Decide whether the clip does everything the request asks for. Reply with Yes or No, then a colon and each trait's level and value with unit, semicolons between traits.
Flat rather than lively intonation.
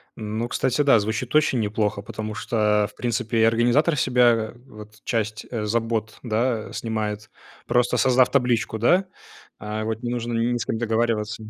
Yes: narrow, 2.2 semitones